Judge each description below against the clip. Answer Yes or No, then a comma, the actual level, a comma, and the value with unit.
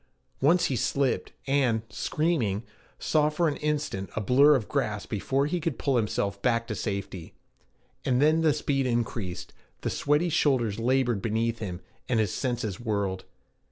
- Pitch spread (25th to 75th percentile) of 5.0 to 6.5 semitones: Yes, average, 5.3 semitones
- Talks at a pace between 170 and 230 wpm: No, average, 160 wpm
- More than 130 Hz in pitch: No, low, 125 Hz